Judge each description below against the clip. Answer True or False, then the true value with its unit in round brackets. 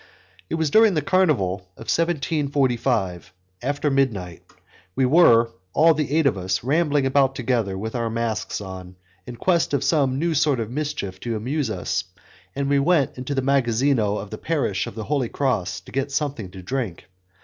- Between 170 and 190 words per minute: True (180 wpm)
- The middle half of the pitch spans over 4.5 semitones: True (5.1 semitones)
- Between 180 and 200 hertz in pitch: False (130 Hz)